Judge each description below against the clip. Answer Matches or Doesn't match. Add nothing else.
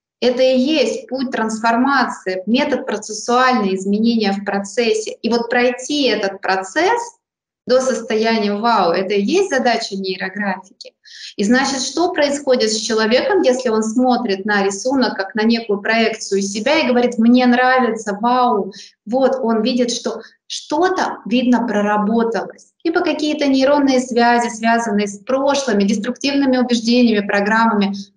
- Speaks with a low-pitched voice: Doesn't match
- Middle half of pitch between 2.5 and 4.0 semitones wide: Matches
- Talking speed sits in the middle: Matches